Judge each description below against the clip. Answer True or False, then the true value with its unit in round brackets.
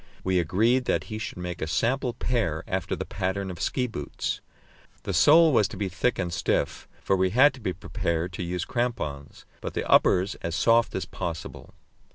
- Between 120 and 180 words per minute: False (195 wpm)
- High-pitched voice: False (95 Hz)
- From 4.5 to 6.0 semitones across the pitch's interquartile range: True (5.2 semitones)